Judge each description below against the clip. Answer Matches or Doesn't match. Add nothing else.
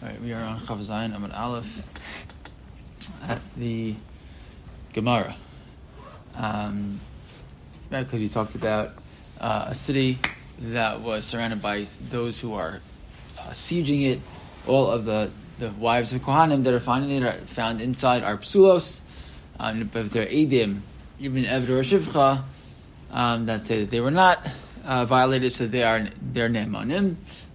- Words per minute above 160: Doesn't match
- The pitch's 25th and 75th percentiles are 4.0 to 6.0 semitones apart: Doesn't match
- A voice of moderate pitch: Doesn't match